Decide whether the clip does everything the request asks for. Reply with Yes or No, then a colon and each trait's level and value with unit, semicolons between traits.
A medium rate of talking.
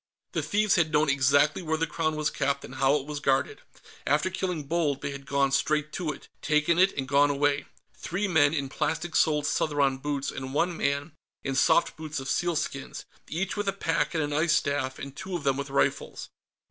No: fast, 210 wpm